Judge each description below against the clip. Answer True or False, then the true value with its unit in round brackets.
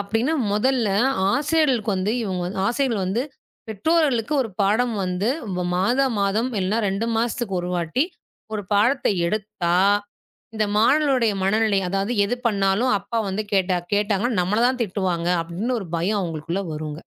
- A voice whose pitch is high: True (210 Hz)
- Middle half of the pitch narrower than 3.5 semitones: False (4.0 semitones)